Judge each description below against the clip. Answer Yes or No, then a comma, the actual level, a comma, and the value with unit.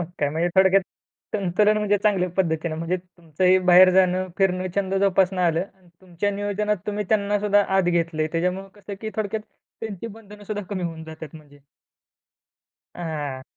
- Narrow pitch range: No, average, 3.0 semitones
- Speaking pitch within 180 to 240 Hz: Yes, medium, 185 Hz